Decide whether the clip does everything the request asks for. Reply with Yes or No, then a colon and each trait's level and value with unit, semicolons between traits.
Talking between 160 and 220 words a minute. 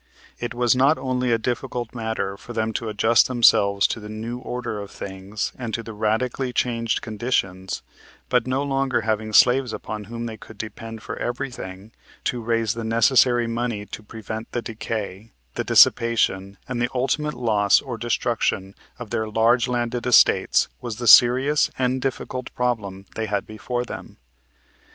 Yes: average, 165 wpm